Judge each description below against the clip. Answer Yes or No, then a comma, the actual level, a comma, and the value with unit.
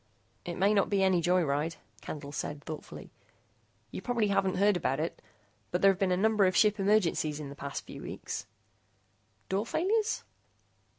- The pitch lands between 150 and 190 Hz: Yes, medium, 185 Hz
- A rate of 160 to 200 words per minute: Yes, average, 170 wpm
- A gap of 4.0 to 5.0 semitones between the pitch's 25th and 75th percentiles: Yes, average, 4.6 semitones